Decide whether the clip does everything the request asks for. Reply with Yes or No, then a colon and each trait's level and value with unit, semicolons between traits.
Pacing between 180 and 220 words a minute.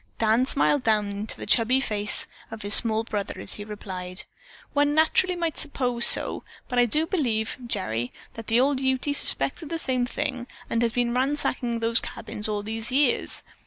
Yes: average, 185 wpm